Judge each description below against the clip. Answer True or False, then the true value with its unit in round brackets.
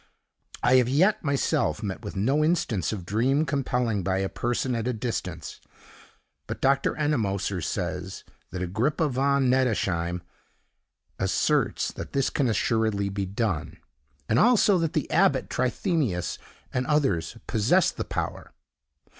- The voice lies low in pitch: True (120 Hz)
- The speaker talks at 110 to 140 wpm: True (135 wpm)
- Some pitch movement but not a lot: False (6.3 semitones)